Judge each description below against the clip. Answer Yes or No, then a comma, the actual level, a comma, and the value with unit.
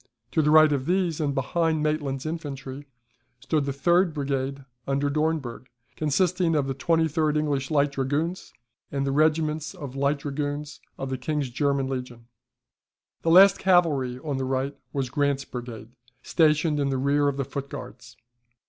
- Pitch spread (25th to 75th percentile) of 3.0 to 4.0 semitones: No, narrow, 2.4 semitones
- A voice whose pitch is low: No, medium, 145 Hz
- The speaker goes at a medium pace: Yes, average, 160 wpm